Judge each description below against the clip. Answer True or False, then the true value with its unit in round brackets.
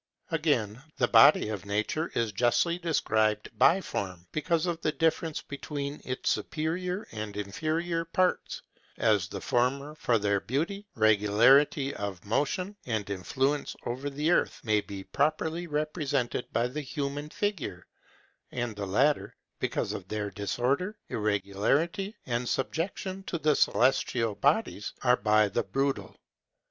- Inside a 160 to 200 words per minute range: False (135 wpm)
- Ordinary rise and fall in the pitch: False (6.7 semitones)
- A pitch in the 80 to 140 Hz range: True (135 Hz)